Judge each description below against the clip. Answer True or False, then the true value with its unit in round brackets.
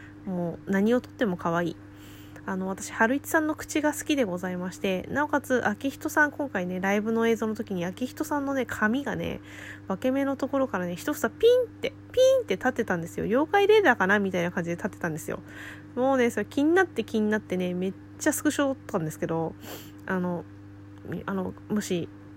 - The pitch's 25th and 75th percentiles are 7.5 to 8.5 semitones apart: True (7.8 semitones)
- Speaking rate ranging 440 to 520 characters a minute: False (400 characters per minute)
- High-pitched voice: True (205 Hz)